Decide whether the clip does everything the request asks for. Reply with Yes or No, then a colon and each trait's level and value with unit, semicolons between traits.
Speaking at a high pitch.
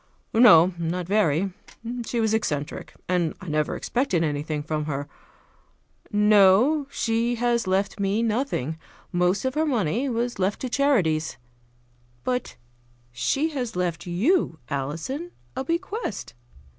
Yes: high, 200 Hz